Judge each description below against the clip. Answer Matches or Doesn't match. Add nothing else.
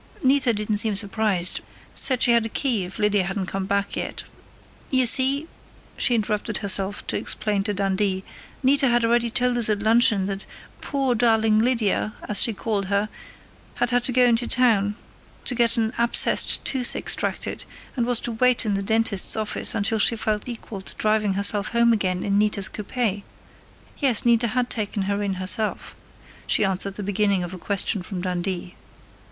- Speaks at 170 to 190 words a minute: Matches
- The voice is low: Doesn't match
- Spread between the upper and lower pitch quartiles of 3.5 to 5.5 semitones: Doesn't match